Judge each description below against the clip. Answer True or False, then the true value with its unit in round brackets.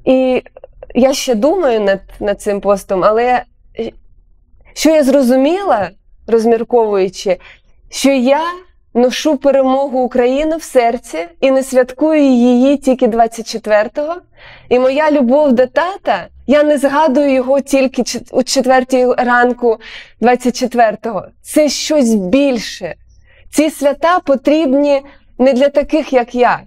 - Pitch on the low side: False (260 Hz)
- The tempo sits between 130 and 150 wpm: False (115 wpm)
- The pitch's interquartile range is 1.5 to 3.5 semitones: True (3.2 semitones)